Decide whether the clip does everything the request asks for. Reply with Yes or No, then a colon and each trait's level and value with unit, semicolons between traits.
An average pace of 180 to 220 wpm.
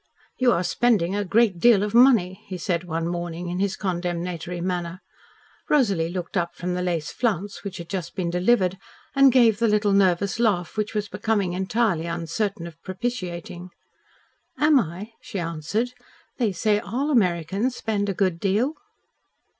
No: average, 160 wpm